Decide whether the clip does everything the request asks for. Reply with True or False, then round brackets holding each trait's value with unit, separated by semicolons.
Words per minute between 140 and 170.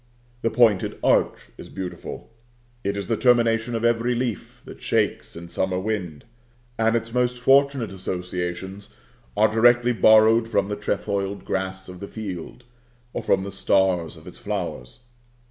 True (150 wpm)